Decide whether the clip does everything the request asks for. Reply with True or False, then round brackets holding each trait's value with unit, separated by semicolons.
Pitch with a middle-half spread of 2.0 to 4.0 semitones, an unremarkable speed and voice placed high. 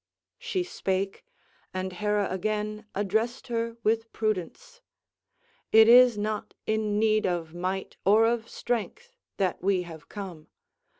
False (3.1 semitones; 125 wpm; 215 Hz)